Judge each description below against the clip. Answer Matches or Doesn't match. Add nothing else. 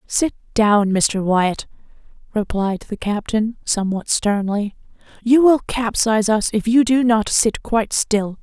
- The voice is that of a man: Doesn't match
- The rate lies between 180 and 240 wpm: Doesn't match